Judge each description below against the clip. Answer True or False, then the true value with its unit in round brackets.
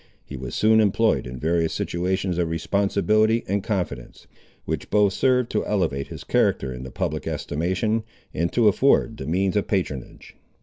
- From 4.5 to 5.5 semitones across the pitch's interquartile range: True (4.8 semitones)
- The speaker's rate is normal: True (165 wpm)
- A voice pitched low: True (95 Hz)